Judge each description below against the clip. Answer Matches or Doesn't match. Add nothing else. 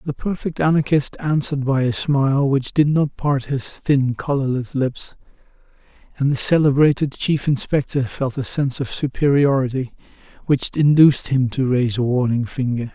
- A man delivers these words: Matches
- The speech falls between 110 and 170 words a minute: Matches